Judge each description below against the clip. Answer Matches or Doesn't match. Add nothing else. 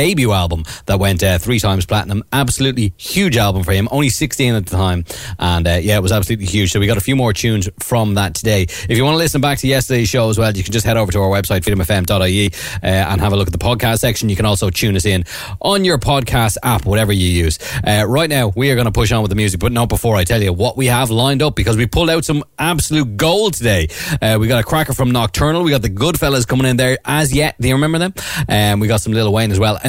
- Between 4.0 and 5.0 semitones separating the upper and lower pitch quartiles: Matches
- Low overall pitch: Matches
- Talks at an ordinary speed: Doesn't match